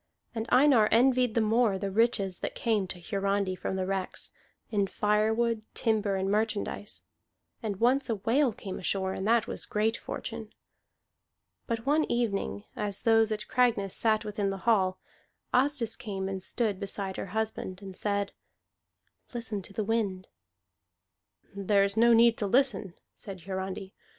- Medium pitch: No, high, 210 Hz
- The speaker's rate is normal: Yes, average, 155 wpm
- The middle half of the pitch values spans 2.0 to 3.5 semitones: Yes, average, 2.8 semitones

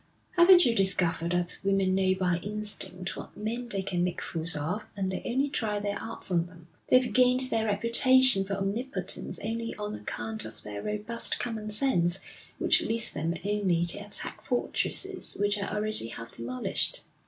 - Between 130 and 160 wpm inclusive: No, average, 170 wpm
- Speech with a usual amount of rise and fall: Yes, average, 4.5 semitones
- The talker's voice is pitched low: No, high, 205 Hz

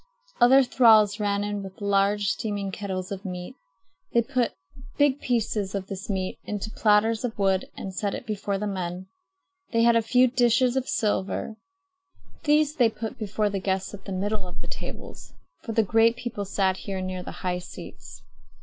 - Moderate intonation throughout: Yes, average, 3.0 semitones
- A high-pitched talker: Yes, high, 205 Hz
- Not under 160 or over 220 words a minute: Yes, average, 180 wpm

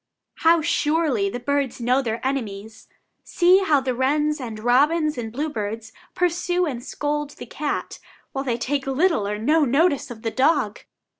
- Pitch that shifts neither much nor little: Yes, average, 4.6 semitones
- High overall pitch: Yes, very high, 270 Hz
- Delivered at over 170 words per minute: No, average, 160 wpm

